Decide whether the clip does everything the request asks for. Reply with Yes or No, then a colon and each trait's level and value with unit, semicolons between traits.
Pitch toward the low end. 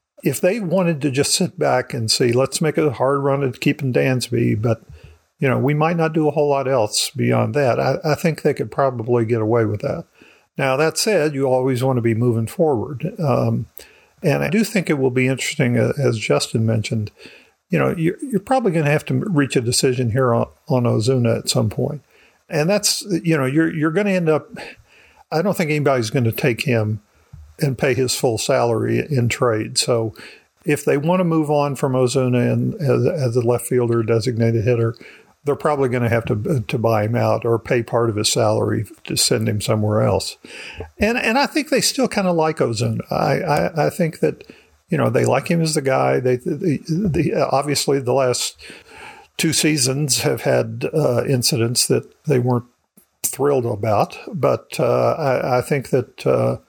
Yes: low, 130 Hz